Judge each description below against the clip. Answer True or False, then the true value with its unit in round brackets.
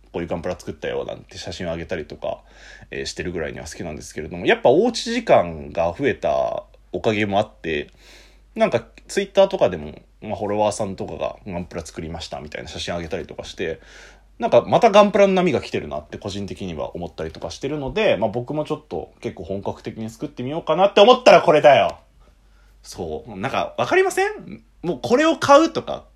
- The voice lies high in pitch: False (130 Hz)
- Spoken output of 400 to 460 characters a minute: True (455 characters per minute)